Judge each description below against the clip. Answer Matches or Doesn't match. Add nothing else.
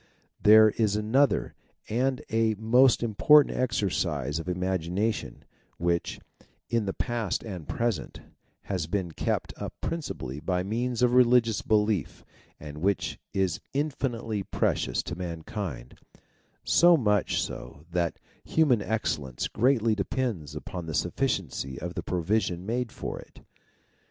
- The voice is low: Matches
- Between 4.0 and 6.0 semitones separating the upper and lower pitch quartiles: Matches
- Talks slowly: Matches